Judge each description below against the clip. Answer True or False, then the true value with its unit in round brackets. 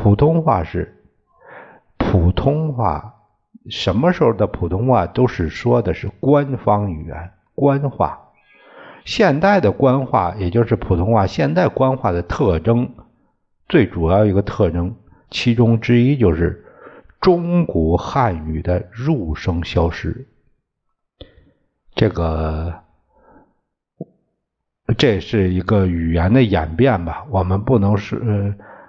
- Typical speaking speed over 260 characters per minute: False (175 characters per minute)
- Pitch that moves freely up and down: True (5.8 semitones)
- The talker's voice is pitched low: True (100 Hz)